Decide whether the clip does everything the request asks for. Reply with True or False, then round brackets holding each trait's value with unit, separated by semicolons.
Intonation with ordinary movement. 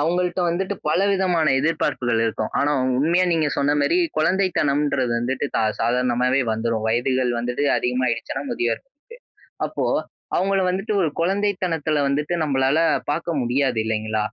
False (5.9 semitones)